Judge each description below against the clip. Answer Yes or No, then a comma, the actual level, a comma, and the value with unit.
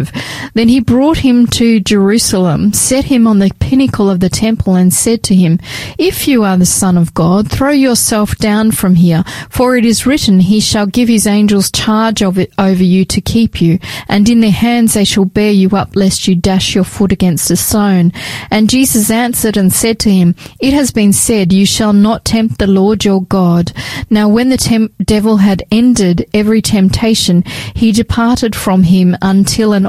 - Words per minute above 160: Yes, average, 195 wpm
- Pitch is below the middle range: No, high, 205 Hz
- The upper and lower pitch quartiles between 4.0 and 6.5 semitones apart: No, average, 3.2 semitones